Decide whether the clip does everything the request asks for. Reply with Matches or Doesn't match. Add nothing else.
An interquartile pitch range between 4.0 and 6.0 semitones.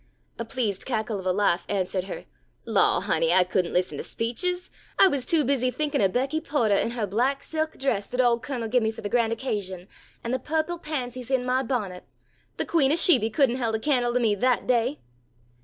Matches